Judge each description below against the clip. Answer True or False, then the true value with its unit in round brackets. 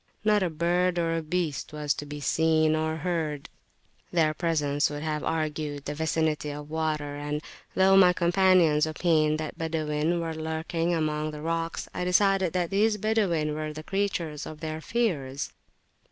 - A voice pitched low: False (160 Hz)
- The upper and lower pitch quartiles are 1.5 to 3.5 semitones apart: True (2.5 semitones)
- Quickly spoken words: False (165 wpm)